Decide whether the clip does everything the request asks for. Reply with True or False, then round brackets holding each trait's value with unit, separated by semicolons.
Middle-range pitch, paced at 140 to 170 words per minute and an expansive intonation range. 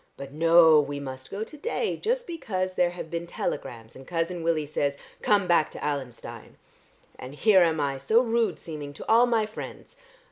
False (165 Hz; 185 wpm; 6.9 semitones)